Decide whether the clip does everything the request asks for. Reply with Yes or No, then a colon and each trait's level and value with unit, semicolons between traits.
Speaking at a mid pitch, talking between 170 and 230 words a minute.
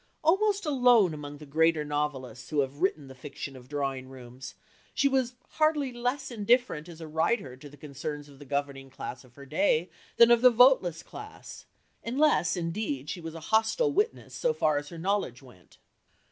Yes: medium, 160 Hz; average, 185 wpm